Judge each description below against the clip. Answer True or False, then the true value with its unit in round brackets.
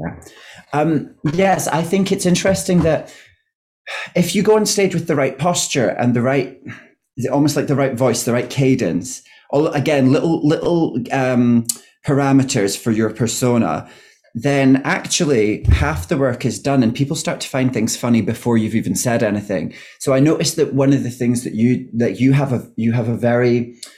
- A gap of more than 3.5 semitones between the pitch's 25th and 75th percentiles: True (4.7 semitones)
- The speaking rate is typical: True (185 wpm)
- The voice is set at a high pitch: False (135 Hz)